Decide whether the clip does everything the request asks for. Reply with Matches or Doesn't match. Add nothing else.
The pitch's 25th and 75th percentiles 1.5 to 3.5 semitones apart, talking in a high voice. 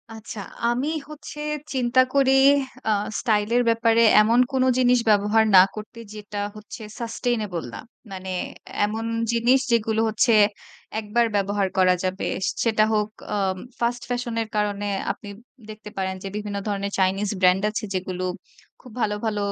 Matches